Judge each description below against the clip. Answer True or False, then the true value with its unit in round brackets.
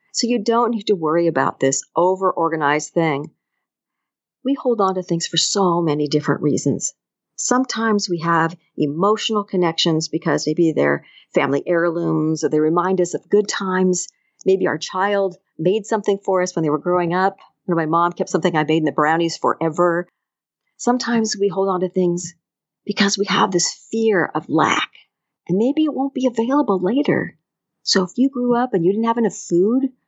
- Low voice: False (185 Hz)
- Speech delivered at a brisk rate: False (185 wpm)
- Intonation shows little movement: False (4.0 semitones)